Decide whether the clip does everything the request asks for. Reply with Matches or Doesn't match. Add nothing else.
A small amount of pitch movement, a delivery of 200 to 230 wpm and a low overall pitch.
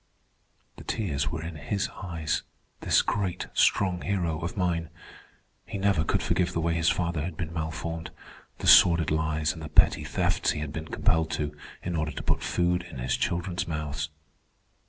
Doesn't match